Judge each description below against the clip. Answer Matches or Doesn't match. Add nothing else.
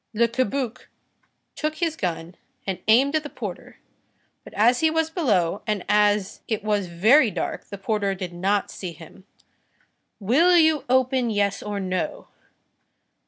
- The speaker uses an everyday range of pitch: Doesn't match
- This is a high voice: Matches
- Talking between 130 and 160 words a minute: Matches